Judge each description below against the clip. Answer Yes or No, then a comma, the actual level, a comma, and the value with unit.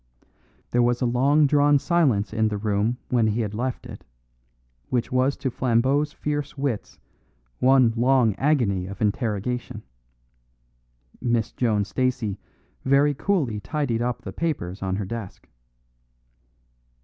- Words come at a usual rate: No, slow, 130 wpm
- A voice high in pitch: No, low, 120 Hz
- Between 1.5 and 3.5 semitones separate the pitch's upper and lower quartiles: No, average, 4.2 semitones